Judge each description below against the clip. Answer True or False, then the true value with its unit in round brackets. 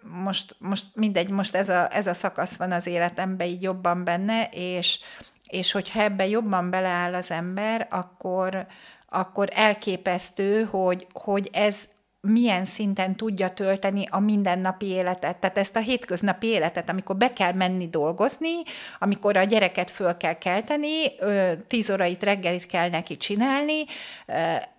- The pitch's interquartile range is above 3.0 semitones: False (2.6 semitones)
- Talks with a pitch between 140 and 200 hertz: True (190 Hz)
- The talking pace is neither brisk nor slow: True (140 wpm)